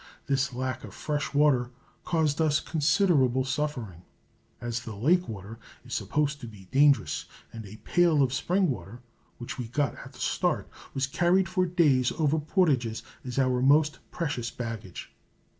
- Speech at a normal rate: Yes, average, 160 wpm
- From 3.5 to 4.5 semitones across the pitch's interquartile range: Yes, average, 4.2 semitones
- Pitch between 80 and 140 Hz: Yes, low, 135 Hz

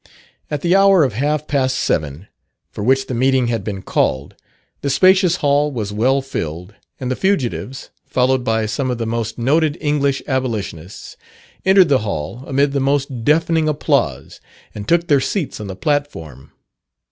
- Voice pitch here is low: Yes, low, 130 Hz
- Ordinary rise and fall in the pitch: Yes, average, 4.7 semitones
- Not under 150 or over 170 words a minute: Yes, average, 165 wpm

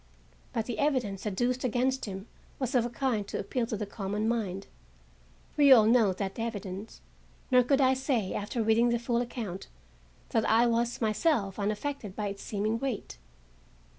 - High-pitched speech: Yes, high, 225 Hz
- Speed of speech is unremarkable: Yes, average, 160 wpm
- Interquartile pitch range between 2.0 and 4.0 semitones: Yes, average, 3.6 semitones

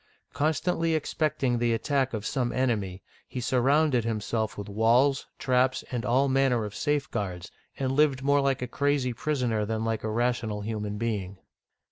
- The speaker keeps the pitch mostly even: No, average, 3.7 semitones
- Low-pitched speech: Yes, low, 125 Hz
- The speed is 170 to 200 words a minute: No, average, 155 wpm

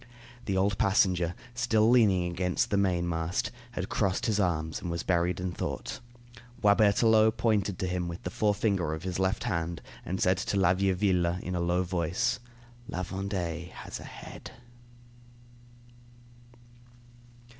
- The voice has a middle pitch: No, very low, 95 Hz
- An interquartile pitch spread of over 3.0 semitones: No, narrow, 2.5 semitones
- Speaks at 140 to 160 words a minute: Yes, average, 145 wpm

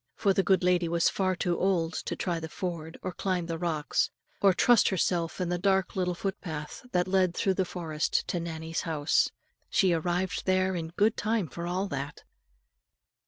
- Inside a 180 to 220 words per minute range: Yes, average, 185 wpm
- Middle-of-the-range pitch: Yes, medium, 180 Hz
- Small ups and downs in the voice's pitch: Yes, narrow, 2.3 semitones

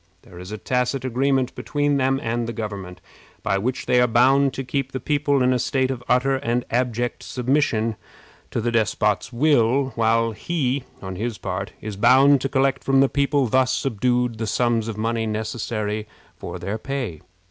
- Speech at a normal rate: Yes, average, 180 wpm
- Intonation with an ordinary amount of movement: Yes, average, 3.3 semitones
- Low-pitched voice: Yes, low, 125 Hz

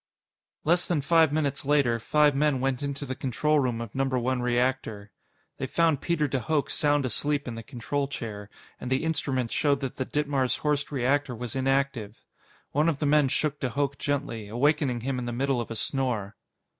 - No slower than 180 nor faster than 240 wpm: Yes, average, 195 wpm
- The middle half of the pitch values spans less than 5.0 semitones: Yes, average, 3.0 semitones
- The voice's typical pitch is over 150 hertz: No, low, 135 Hz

